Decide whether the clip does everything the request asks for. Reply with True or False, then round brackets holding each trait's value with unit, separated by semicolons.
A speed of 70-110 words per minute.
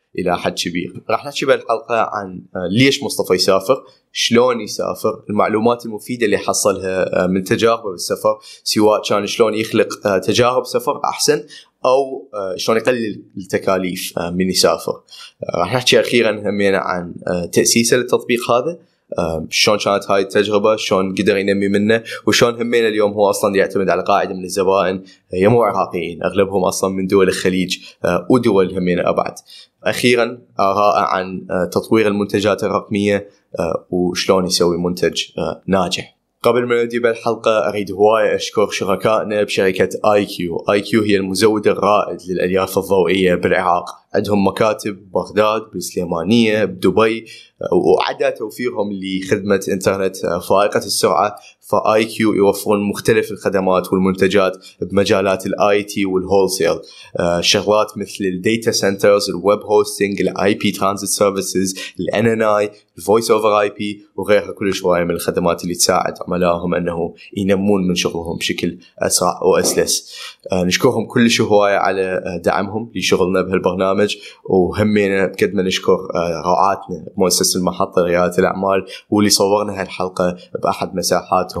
False (125 wpm)